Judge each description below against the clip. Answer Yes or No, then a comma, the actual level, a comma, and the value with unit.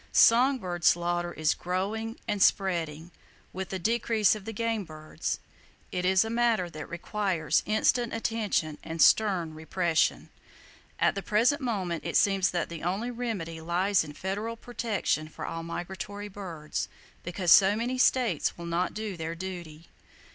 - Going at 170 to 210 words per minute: No, average, 150 wpm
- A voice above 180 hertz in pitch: Yes, high, 190 Hz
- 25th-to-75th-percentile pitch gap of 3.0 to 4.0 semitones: No, average, 4.5 semitones